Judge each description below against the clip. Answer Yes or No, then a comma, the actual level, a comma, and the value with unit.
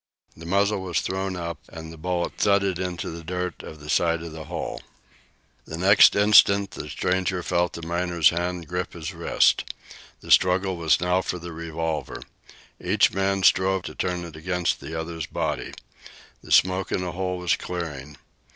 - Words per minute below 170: No, average, 175 wpm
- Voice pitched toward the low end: Yes, very low, 90 Hz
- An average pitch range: No, narrow, 2.0 semitones